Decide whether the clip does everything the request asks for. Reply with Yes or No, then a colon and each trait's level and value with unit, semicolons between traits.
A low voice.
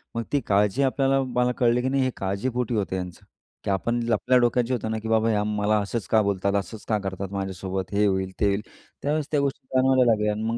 Yes: low, 110 Hz